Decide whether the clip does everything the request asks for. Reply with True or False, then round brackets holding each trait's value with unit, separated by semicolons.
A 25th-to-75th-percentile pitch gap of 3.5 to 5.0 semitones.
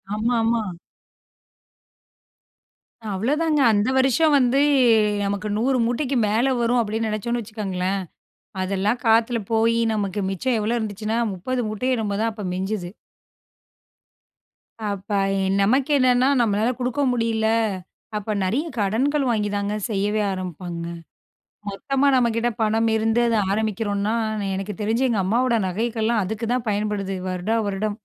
False (2.9 semitones)